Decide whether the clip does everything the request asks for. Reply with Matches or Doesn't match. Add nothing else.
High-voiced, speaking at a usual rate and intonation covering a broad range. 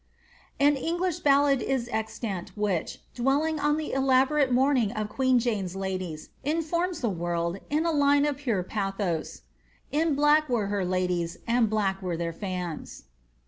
Matches